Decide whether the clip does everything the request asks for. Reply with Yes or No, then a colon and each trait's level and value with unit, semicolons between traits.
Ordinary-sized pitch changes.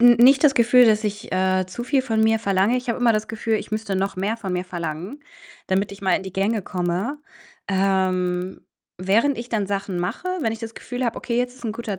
Yes: average, 3.9 semitones